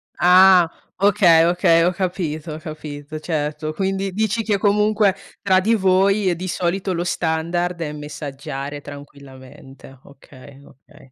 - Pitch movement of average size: Yes, average, 4.4 semitones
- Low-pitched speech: No, medium, 170 Hz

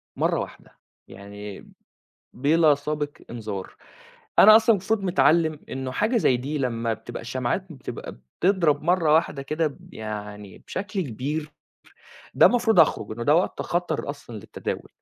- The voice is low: No, medium, 145 Hz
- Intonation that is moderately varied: No, wide, 6.5 semitones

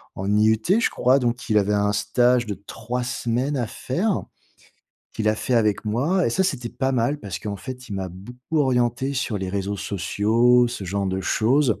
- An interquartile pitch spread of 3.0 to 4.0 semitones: Yes, average, 3.7 semitones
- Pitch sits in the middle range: No, low, 120 Hz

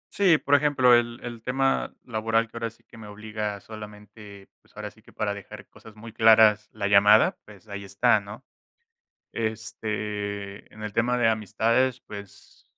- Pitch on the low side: Yes, low, 110 Hz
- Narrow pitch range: Yes, narrow, 2.1 semitones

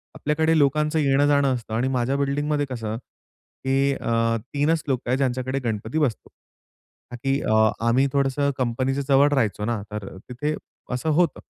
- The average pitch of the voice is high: No, low, 135 Hz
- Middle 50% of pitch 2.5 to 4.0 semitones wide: Yes, average, 3.4 semitones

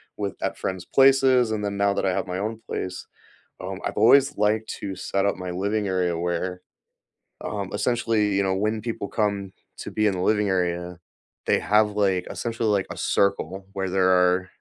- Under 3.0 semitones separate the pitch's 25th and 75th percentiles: Yes, narrow, 2.6 semitones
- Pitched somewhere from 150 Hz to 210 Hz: No, low, 100 Hz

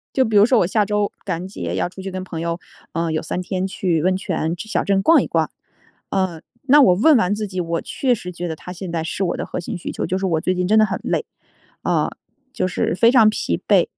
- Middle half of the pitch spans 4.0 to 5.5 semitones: No, average, 3.2 semitones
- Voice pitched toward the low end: No, medium, 185 Hz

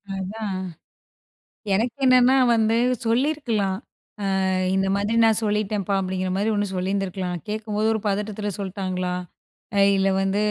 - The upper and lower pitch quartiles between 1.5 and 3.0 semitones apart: Yes, narrow, 2.4 semitones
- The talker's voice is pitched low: No, high, 205 Hz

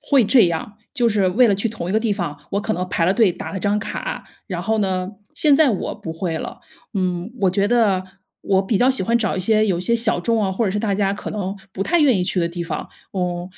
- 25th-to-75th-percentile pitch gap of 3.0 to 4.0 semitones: Yes, average, 3.6 semitones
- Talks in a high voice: Yes, high, 200 Hz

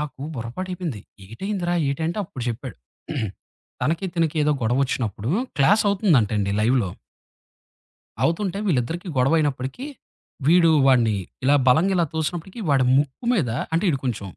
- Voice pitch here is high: No, medium, 150 Hz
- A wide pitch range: Yes, wide, 5.8 semitones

